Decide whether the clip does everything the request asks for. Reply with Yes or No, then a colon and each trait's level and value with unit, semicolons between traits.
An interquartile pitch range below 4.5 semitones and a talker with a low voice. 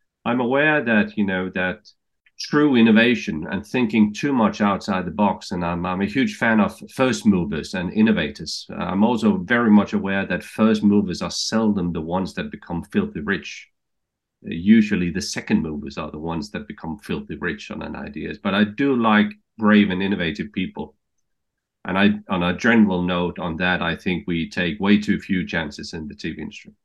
No: average, 4.9 semitones; low, 105 Hz